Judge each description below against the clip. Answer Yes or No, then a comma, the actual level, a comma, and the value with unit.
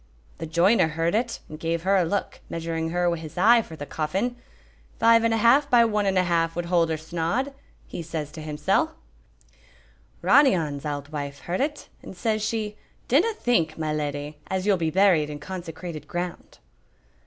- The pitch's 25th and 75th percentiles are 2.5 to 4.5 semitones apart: No, average, 5.0 semitones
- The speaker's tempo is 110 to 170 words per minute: No, average, 190 wpm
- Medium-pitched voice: Yes, medium, 170 Hz